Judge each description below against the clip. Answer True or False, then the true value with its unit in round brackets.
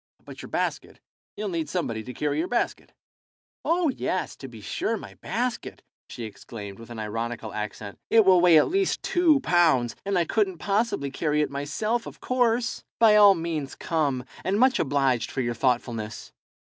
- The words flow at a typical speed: True (175 wpm)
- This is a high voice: False (160 Hz)